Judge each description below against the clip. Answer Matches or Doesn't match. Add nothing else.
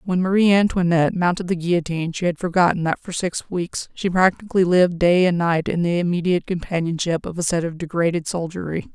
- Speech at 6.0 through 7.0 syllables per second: Matches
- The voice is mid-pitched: Matches